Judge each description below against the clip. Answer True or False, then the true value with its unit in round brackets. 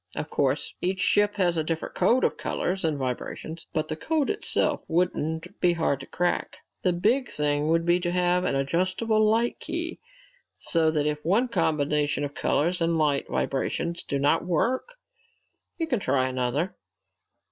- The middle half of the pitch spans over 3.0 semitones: True (3.9 semitones)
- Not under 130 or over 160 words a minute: False (170 wpm)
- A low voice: False (165 Hz)